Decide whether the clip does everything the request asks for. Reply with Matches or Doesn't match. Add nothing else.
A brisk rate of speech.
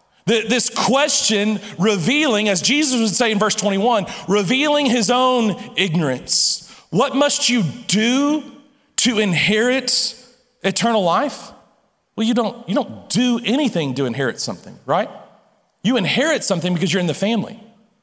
Doesn't match